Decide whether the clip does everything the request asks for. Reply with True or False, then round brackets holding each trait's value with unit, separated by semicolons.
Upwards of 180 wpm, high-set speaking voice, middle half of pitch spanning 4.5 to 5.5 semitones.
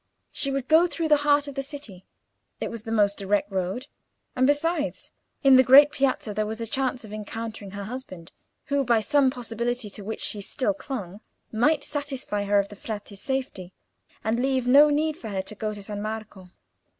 True (200 wpm; 235 Hz; 5.1 semitones)